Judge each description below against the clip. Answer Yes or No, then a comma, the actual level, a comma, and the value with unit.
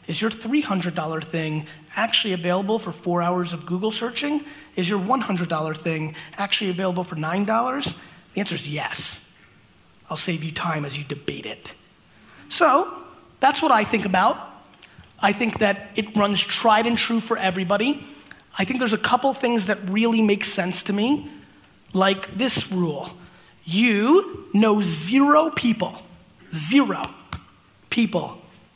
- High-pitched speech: Yes, high, 200 Hz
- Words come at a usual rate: Yes, average, 145 wpm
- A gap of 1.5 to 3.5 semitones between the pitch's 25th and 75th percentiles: No, average, 4.8 semitones